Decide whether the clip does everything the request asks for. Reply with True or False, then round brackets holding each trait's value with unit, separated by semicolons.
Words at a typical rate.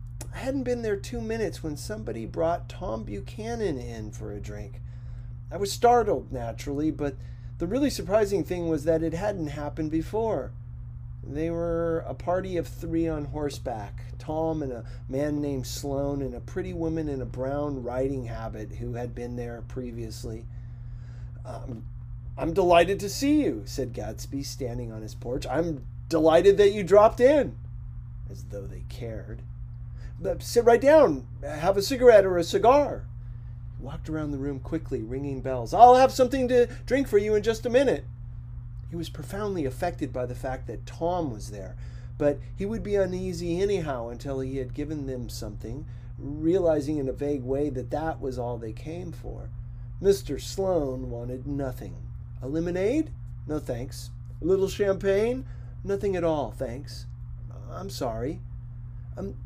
True (160 wpm)